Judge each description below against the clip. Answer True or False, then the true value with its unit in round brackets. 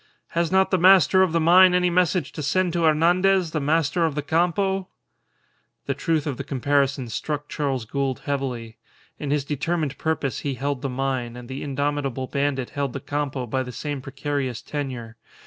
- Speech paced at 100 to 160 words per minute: False (180 wpm)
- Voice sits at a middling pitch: True (145 Hz)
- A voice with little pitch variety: False (3.7 semitones)